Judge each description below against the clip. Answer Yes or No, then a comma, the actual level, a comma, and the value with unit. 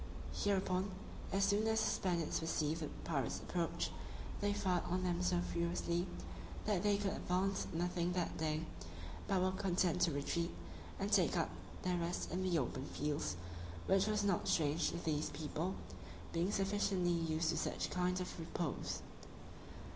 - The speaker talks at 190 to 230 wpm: No, average, 155 wpm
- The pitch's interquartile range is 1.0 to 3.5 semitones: Yes, narrow, 2.6 semitones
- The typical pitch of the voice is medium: Yes, medium, 175 Hz